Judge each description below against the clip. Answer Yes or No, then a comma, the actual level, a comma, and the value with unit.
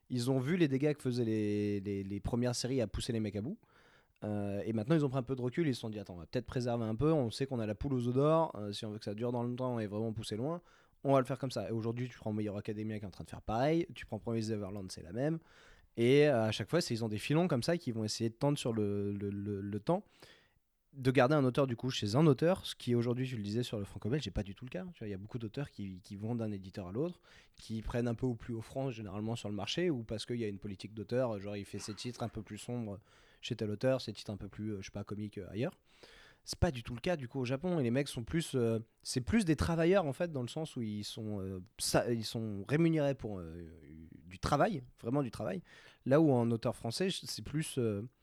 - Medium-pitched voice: No, low, 115 Hz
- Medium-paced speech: No, fast, 295 wpm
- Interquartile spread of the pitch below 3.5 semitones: No, average, 4.3 semitones